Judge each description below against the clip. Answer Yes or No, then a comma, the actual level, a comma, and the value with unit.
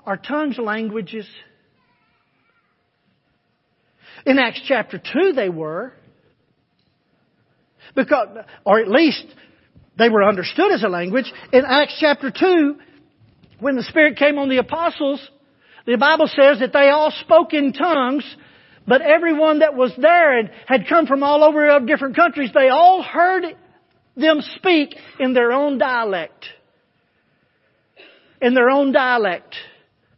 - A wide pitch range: No, average, 3.5 semitones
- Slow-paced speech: Yes, slow, 130 wpm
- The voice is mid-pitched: No, very high, 285 Hz